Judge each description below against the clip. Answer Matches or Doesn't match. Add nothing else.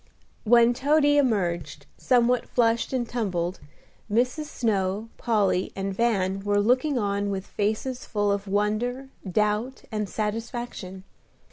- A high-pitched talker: Matches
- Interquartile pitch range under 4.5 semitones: Matches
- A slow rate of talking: Matches